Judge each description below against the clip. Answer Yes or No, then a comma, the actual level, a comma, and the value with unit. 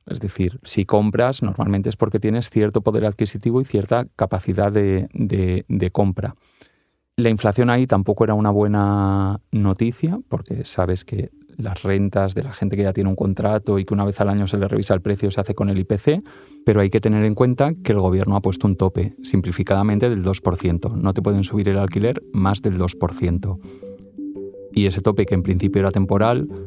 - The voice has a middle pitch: No, low, 100 Hz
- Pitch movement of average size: No, narrow, 2.1 semitones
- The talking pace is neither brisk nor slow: No, fast, 200 wpm